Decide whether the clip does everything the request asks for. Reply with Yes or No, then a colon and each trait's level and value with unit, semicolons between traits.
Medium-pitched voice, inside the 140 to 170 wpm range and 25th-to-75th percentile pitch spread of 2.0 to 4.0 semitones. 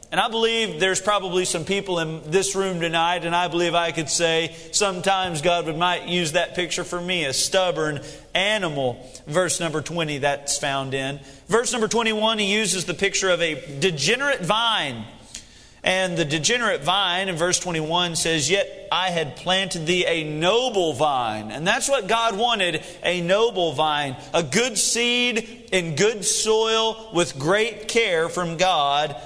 Yes: medium, 175 Hz; average, 165 wpm; average, 3.6 semitones